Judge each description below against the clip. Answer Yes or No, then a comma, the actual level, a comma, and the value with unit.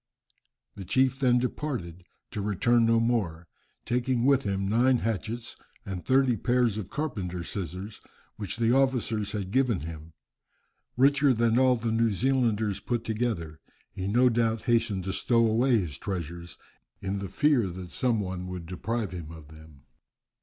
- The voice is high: No, low, 110 Hz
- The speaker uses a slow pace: No, average, 155 wpm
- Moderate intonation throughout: Yes, average, 4.8 semitones